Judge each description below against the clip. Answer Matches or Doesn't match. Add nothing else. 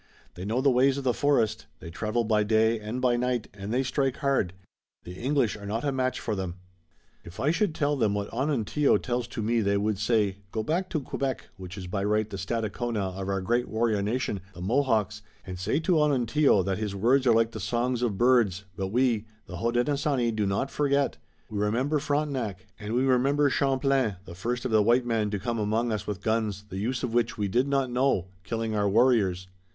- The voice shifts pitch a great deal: Doesn't match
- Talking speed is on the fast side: Matches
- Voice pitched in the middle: Doesn't match